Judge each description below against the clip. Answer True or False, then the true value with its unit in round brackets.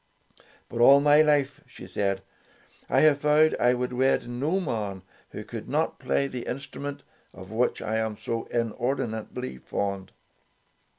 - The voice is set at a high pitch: False (125 Hz)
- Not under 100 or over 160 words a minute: True (150 wpm)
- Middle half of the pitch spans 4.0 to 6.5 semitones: True (4.5 semitones)